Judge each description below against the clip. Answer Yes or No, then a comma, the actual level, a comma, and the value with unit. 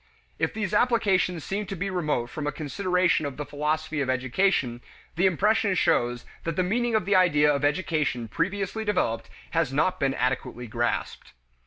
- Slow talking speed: No, average, 170 wpm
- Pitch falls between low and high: Yes, medium, 160 Hz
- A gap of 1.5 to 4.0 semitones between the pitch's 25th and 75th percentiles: No, wide, 5.6 semitones